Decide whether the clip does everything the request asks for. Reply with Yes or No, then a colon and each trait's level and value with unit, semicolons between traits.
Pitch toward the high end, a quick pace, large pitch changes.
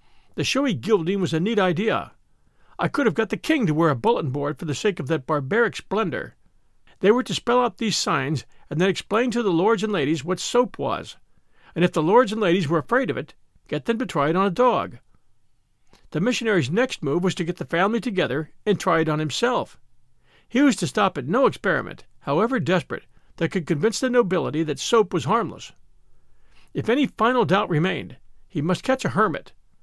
Yes: high, 195 Hz; fast, 210 wpm; wide, 5.7 semitones